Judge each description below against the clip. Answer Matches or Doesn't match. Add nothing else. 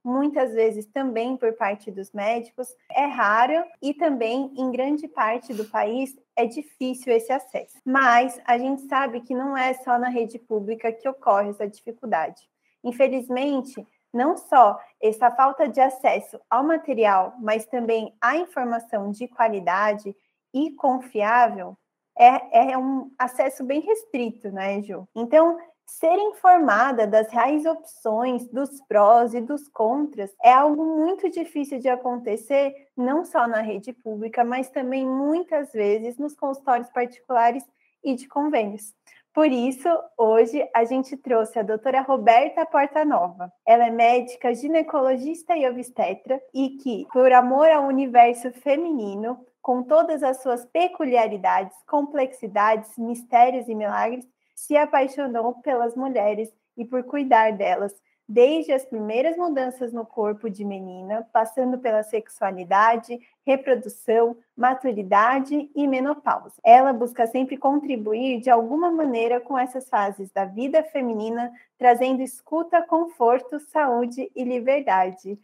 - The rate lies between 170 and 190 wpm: Doesn't match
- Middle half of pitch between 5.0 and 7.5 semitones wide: Doesn't match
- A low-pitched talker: Doesn't match